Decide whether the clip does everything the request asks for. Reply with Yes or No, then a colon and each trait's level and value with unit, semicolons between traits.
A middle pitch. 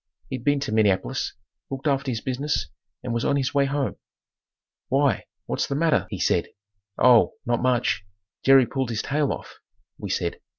No: low, 130 Hz